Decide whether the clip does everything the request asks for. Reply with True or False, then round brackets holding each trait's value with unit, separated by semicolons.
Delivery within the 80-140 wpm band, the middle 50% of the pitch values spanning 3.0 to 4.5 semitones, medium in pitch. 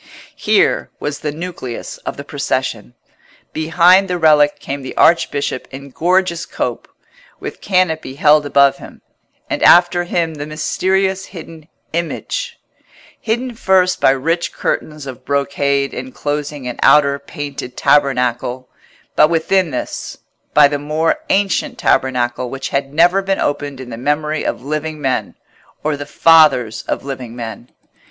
True (135 wpm; 3.8 semitones; 150 Hz)